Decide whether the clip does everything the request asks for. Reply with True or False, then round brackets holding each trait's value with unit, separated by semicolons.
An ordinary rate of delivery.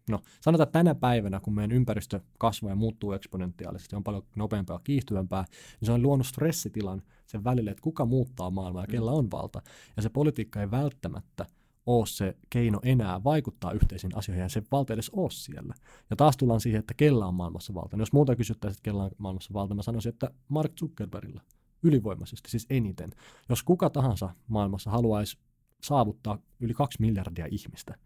False (185 wpm)